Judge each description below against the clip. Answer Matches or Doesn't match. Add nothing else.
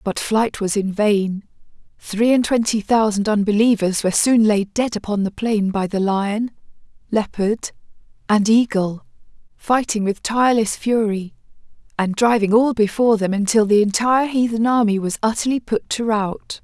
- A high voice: Matches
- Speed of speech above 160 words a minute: Doesn't match